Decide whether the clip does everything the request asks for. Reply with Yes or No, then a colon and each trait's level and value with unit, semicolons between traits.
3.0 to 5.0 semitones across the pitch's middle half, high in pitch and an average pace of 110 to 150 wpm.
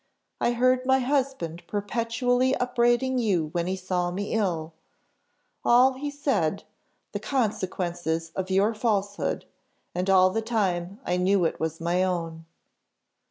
No: wide, 5.6 semitones; high, 200 Hz; slow, 135 wpm